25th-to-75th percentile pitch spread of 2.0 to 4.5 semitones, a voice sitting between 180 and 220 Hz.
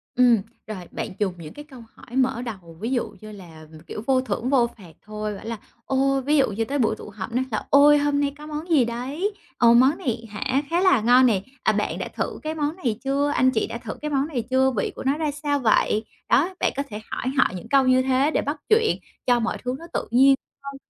No: average, 4.2 semitones; very high, 255 Hz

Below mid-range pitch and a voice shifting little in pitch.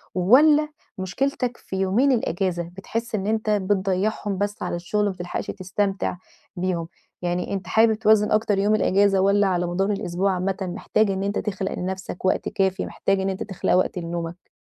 No: high, 195 Hz; narrow, 2.3 semitones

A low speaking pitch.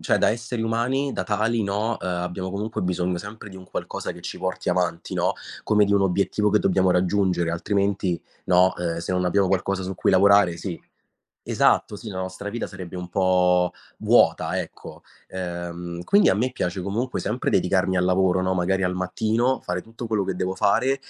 Yes: very low, 95 Hz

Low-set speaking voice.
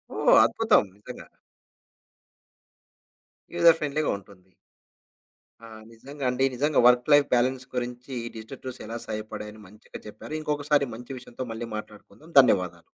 Yes: low, 125 Hz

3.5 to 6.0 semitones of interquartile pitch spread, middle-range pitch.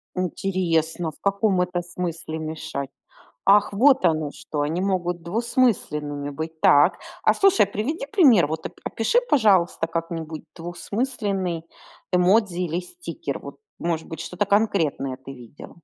Yes: average, 4.1 semitones; medium, 175 Hz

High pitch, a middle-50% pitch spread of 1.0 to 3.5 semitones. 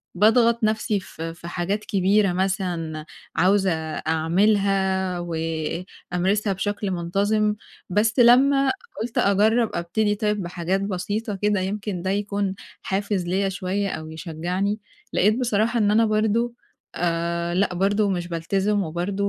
Yes: high, 195 Hz; average, 3.1 semitones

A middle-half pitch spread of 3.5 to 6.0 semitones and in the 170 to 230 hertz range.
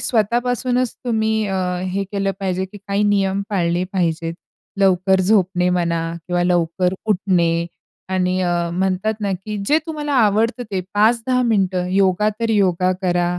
No: average, 3.0 semitones; high, 190 Hz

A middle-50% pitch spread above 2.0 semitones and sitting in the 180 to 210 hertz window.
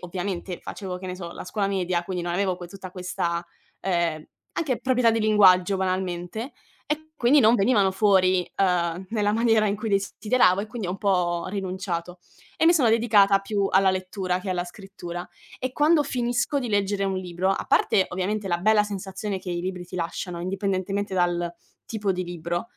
Yes: average, 2.8 semitones; high, 190 Hz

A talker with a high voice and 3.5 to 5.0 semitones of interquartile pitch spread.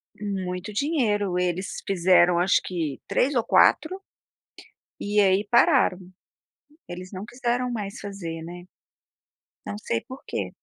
Yes: high, 195 Hz; average, 4.6 semitones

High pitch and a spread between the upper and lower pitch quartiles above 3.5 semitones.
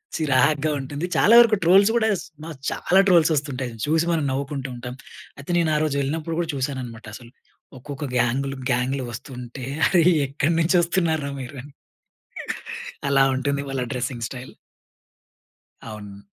No: medium, 140 Hz; average, 3.9 semitones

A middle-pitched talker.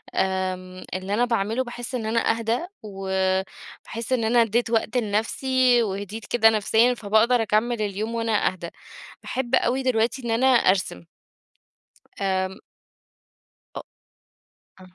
No: high, 225 Hz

